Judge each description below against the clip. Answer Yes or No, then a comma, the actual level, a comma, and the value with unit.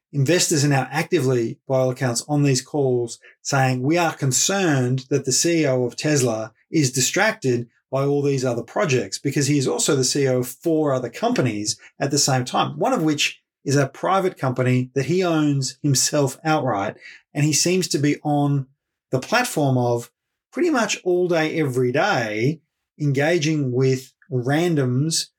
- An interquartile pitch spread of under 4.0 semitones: Yes, average, 3.3 semitones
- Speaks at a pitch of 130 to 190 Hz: Yes, medium, 140 Hz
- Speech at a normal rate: Yes, average, 165 wpm